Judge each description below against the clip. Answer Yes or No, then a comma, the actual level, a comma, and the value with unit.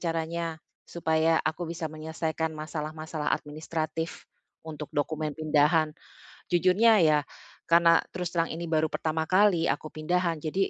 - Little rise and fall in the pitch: Yes, narrow, 1.5 semitones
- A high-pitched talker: No, medium, 160 Hz